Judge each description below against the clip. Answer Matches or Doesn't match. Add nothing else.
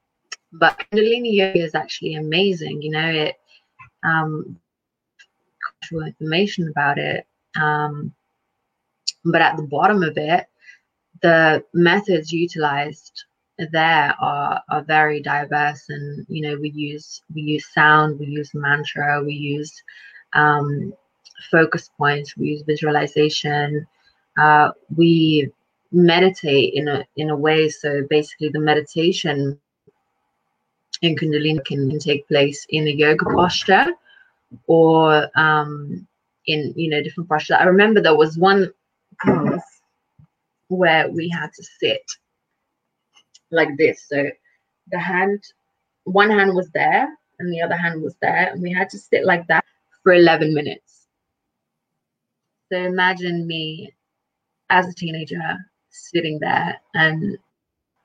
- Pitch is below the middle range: Doesn't match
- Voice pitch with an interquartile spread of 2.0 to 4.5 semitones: Matches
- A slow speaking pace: Matches